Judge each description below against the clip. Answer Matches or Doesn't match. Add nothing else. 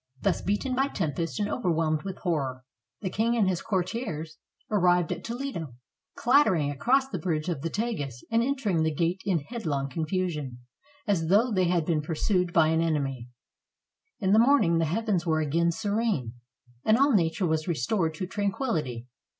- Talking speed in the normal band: Matches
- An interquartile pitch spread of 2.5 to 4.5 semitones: Doesn't match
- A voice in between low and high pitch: Matches